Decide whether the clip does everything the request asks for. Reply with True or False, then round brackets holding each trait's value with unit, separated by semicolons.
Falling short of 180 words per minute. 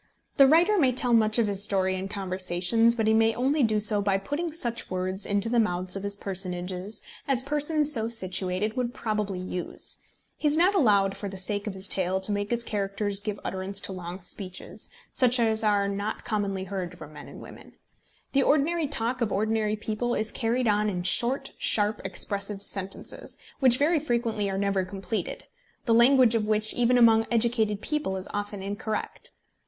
False (190 wpm)